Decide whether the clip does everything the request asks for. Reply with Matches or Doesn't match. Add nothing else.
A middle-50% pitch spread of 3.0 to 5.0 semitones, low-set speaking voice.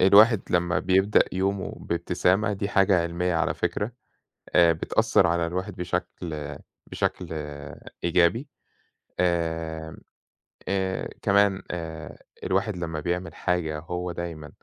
Doesn't match